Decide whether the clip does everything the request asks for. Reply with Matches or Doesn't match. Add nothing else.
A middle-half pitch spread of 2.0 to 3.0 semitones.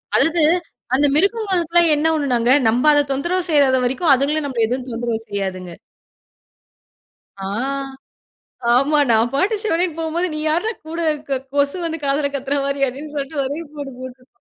Doesn't match